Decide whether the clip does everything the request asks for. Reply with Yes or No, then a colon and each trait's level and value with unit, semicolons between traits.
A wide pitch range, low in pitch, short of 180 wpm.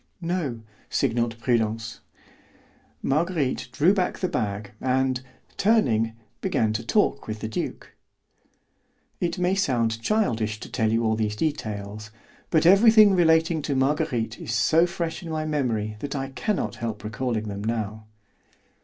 Yes: wide, 6.6 semitones; low, 125 Hz; average, 145 wpm